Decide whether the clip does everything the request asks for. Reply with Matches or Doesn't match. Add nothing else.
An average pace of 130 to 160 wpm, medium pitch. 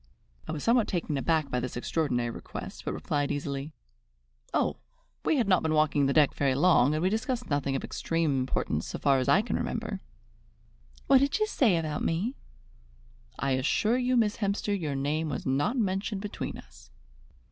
Doesn't match